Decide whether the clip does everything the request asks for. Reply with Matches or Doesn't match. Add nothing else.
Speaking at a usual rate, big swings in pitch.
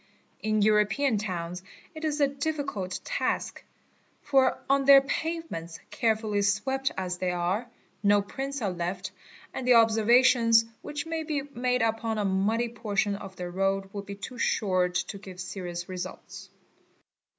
Matches